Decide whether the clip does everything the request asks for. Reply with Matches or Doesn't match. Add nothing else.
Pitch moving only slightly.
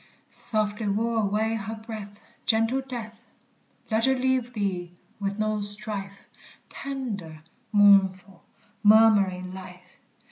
Matches